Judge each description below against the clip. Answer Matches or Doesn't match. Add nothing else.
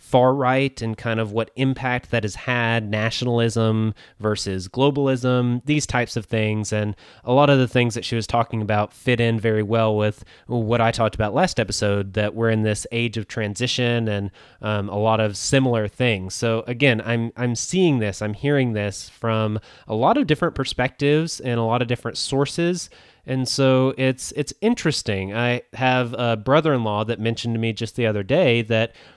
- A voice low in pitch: Matches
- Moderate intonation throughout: Matches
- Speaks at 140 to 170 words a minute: Doesn't match